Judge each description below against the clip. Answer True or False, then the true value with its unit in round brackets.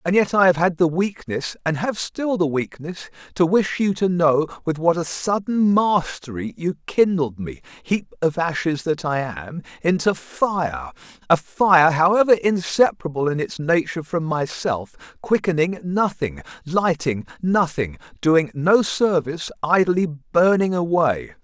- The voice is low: False (165 Hz)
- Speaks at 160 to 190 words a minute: False (145 wpm)